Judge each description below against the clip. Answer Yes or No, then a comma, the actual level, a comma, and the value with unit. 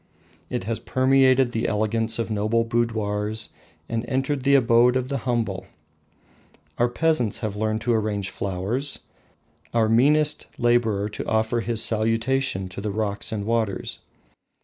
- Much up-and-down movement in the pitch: No, narrow, 2.5 semitones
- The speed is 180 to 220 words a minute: No, average, 140 wpm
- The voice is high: No, low, 115 Hz